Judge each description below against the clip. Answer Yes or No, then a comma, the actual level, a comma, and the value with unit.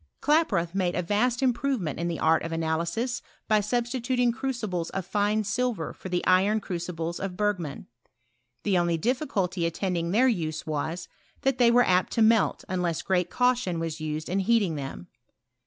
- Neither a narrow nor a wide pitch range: No, wide, 5.7 semitones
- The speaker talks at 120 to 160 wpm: No, average, 170 wpm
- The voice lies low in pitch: No, high, 190 Hz